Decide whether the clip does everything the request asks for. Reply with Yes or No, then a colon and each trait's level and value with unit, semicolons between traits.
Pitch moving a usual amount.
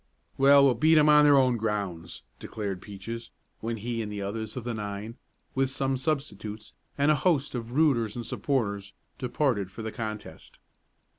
Yes: average, 4.5 semitones